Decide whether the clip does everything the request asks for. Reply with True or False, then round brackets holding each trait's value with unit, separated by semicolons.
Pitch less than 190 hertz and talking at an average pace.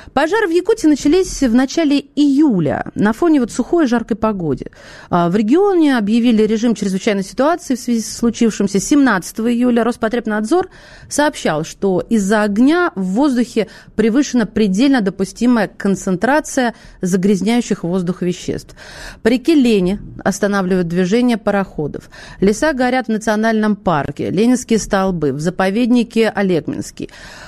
False (225 Hz; 120 wpm)